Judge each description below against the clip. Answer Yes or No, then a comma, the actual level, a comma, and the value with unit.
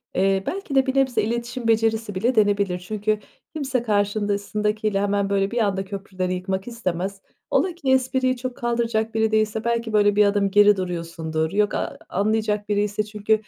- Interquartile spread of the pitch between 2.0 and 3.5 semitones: Yes, average, 2.7 semitones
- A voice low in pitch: No, high, 210 Hz